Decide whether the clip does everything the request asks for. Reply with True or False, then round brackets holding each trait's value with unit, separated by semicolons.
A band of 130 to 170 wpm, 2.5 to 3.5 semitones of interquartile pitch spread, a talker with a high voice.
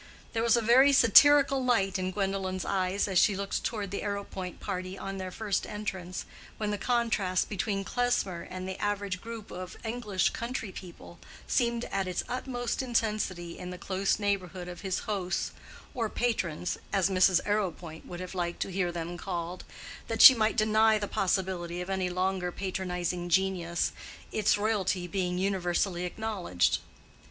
True (160 wpm; 2.9 semitones; 195 Hz)